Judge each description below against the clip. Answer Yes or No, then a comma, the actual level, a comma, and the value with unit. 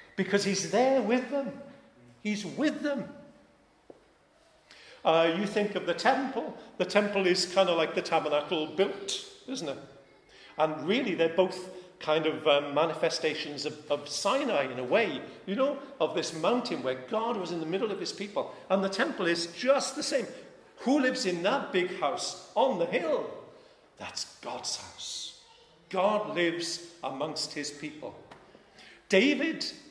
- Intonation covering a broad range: Yes, wide, 8.8 semitones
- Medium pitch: No, high, 195 Hz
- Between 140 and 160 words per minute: Yes, average, 155 wpm